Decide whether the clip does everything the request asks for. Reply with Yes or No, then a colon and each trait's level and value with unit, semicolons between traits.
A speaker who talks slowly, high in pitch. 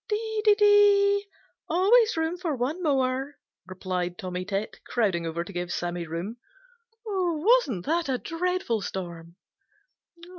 Yes: slow, 125 wpm; very high, 275 Hz